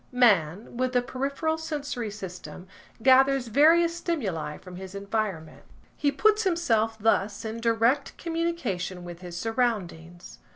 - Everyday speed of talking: No, slow, 125 wpm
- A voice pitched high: Yes, high, 230 Hz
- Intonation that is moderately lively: No, wide, 6.9 semitones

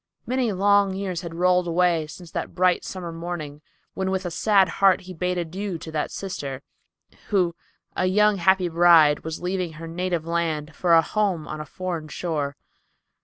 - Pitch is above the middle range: No, medium, 175 Hz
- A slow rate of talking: No, average, 175 wpm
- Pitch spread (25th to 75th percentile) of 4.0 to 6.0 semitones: No, narrow, 2.5 semitones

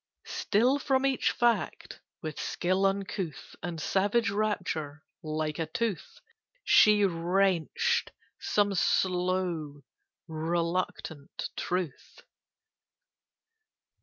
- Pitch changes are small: No, average, 4.3 semitones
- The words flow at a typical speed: No, slow, 80 wpm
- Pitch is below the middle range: No, medium, 185 Hz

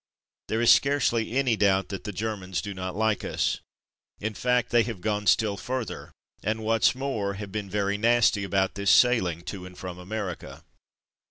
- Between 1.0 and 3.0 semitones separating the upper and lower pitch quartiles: Yes, average, 2.7 semitones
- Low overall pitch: Yes, low, 105 Hz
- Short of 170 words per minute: No, average, 180 wpm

